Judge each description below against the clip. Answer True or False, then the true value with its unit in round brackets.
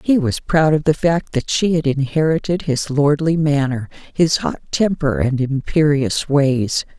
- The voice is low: False (150 Hz)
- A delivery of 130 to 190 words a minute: True (165 wpm)